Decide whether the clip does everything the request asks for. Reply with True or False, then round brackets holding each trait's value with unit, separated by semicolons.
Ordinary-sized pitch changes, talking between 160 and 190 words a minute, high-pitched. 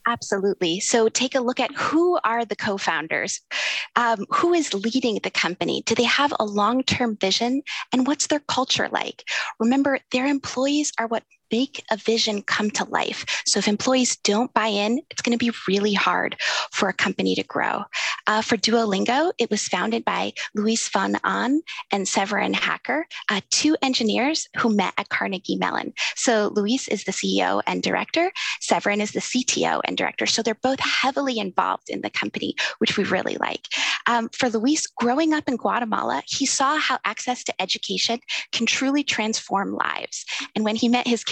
True (4.0 semitones; 180 wpm; 240 Hz)